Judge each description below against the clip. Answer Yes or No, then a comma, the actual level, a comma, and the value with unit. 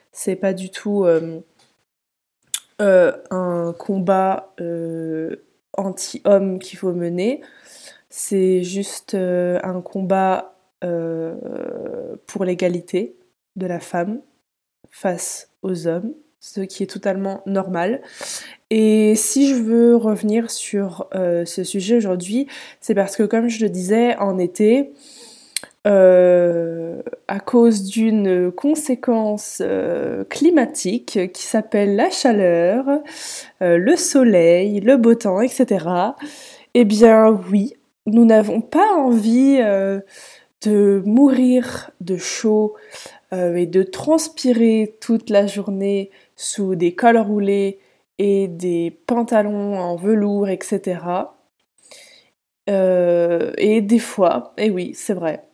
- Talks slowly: Yes, slow, 115 wpm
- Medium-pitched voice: No, high, 205 Hz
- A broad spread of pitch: No, average, 4.1 semitones